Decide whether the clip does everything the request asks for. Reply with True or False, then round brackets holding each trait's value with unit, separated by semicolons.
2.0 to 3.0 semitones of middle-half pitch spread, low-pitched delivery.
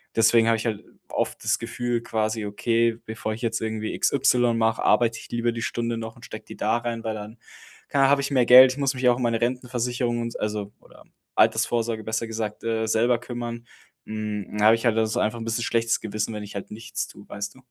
False (1.5 semitones; 115 Hz)